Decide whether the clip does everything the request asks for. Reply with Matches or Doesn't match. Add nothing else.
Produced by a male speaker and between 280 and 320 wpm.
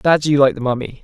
Matches